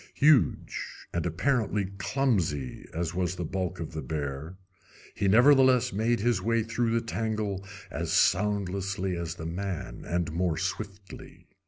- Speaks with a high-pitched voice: No, very low, 95 Hz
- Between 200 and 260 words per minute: No, average, 140 wpm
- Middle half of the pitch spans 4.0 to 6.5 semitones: Yes, average, 4.7 semitones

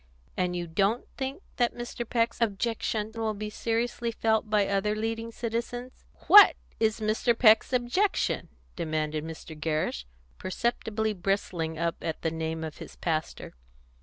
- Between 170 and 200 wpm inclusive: No, average, 140 wpm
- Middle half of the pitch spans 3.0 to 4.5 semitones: No, wide, 5.5 semitones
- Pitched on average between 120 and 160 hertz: No, high, 215 Hz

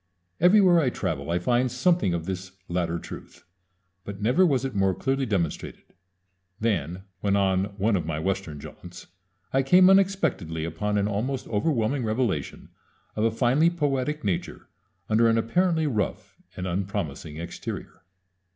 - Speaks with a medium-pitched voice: No, low, 105 Hz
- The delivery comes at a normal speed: Yes, average, 145 wpm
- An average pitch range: No, wide, 6.8 semitones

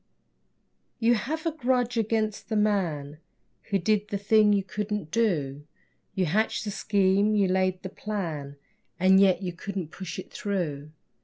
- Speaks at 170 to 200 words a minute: No, average, 155 wpm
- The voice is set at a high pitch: Yes, high, 200 Hz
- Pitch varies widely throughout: No, average, 3.0 semitones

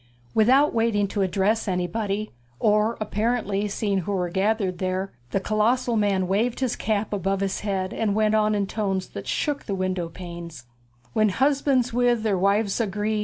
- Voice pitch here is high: Yes, high, 205 Hz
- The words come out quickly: No, average, 170 wpm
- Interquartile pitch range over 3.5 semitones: No, narrow, 2.6 semitones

